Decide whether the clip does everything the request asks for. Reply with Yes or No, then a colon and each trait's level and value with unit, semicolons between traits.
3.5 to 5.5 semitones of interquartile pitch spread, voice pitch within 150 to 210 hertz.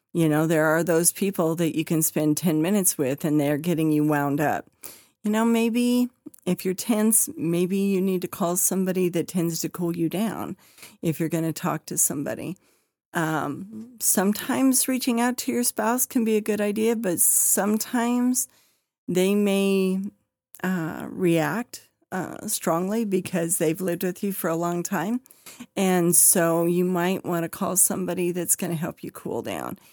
Yes: average, 4.5 semitones; medium, 185 Hz